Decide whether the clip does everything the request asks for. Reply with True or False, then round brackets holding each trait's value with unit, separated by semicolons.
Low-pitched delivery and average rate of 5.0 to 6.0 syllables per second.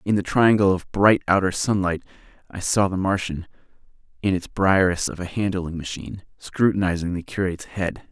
True (95 Hz; 5.3 syllables/s)